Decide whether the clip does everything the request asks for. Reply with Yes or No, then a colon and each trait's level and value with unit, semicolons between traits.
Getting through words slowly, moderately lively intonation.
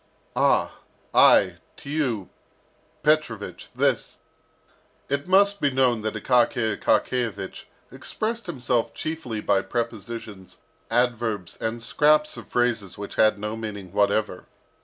Yes: slow, 115 wpm; average, 4.3 semitones